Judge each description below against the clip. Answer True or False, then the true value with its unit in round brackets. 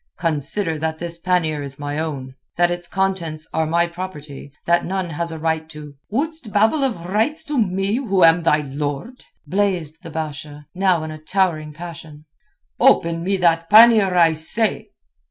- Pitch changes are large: False (3.8 semitones)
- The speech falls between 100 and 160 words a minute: False (170 wpm)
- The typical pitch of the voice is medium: True (170 Hz)